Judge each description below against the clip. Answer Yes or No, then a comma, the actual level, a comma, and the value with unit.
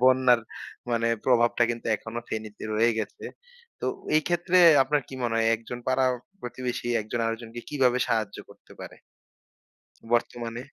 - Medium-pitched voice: No, low, 120 Hz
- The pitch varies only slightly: Yes, narrow, 2.1 semitones